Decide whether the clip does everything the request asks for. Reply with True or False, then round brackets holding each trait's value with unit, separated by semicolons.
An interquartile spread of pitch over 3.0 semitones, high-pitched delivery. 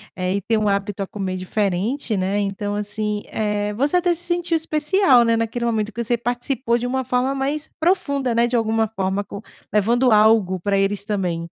True (4.0 semitones; 220 Hz)